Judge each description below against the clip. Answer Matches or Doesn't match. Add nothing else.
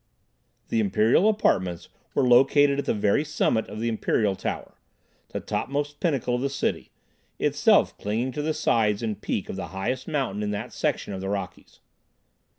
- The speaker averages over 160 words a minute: Matches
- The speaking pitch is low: Matches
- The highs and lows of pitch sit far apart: Matches